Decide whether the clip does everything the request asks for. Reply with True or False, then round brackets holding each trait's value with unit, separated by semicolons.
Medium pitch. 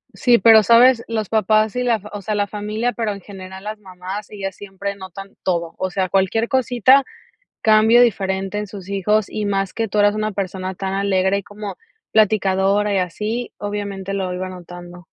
False (200 Hz)